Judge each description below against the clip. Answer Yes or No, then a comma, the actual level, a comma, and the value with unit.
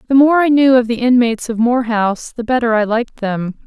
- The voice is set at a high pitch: Yes, high, 240 Hz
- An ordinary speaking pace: No, fast, 245 wpm